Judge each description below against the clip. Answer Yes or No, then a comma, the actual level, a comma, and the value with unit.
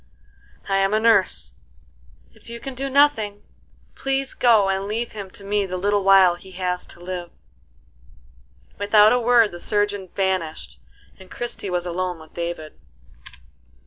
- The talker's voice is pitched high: Yes, high, 195 Hz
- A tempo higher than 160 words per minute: No, average, 150 wpm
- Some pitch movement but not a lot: Yes, average, 3.3 semitones